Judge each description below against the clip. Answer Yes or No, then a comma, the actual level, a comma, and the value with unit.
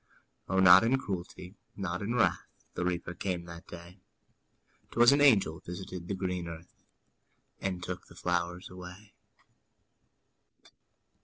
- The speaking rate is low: Yes, slow, 130 wpm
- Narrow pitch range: Yes, narrow, 2.1 semitones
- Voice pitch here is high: No, very low, 90 Hz